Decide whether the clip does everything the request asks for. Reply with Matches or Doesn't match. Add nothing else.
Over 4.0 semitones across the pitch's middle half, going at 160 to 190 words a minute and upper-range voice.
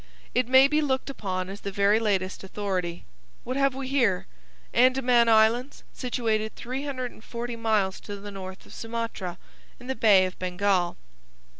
Doesn't match